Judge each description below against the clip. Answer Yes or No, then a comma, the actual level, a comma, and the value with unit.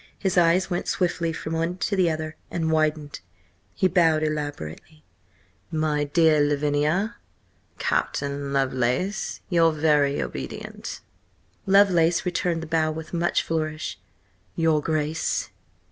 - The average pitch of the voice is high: No, medium, 160 Hz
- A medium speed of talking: No, slow, 115 wpm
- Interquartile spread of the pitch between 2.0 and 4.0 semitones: Yes, narrow, 2.5 semitones